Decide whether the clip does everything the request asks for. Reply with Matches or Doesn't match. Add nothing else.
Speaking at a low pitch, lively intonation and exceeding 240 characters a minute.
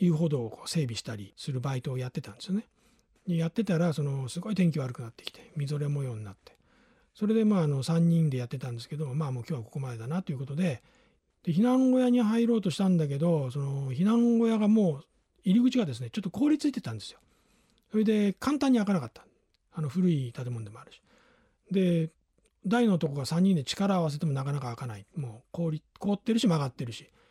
Doesn't match